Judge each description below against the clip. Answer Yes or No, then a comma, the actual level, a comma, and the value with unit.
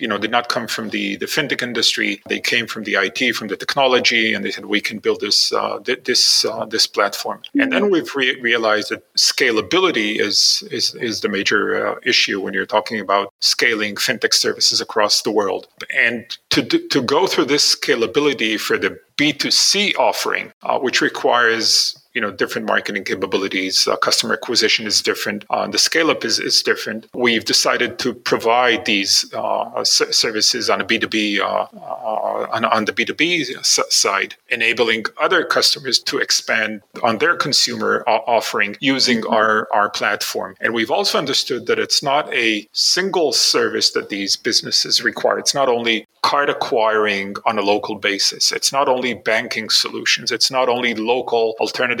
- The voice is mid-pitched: No, low, 120 Hz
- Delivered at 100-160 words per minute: No, average, 175 wpm